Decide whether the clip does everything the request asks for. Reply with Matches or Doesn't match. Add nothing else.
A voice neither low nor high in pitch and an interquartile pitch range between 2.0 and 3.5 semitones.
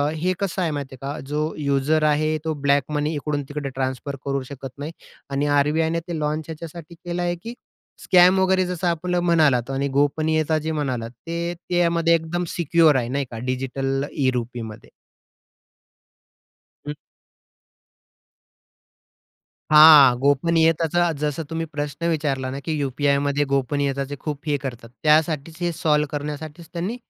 Matches